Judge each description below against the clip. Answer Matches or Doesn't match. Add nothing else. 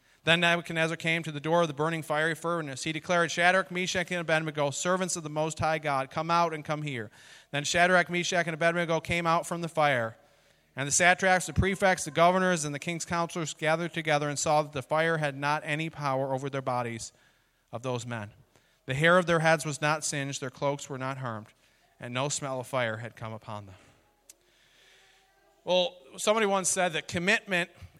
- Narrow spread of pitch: Doesn't match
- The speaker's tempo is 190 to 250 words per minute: Matches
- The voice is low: Doesn't match